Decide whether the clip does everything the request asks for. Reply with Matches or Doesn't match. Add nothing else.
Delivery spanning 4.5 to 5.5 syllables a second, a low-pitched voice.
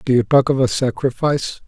Doesn't match